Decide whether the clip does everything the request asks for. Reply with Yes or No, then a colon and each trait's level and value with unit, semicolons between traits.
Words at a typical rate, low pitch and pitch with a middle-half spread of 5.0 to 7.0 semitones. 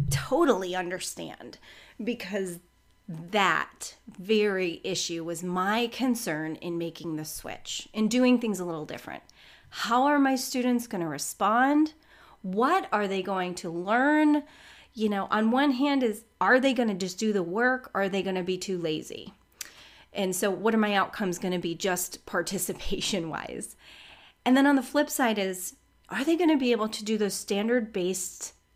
No: average, 175 wpm; high, 205 Hz; average, 5.3 semitones